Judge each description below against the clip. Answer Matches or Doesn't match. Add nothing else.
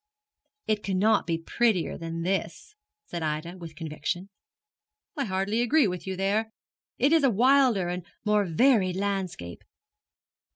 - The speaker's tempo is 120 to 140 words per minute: Matches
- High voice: Matches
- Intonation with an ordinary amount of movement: Matches